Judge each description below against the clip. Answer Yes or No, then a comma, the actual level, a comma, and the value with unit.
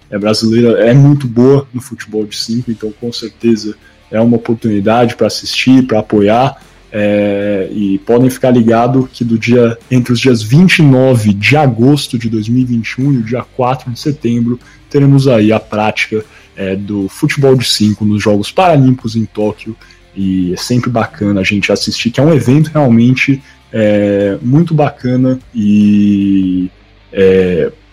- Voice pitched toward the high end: No, low, 115 Hz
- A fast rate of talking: No, average, 155 wpm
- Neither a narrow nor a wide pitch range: Yes, average, 3.6 semitones